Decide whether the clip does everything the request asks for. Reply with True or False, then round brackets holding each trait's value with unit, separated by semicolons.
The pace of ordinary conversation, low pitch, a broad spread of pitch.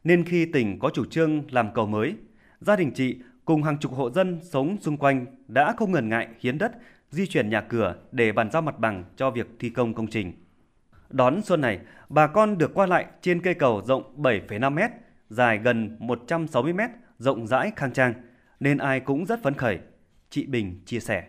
True (200 wpm; 130 Hz; 5.9 semitones)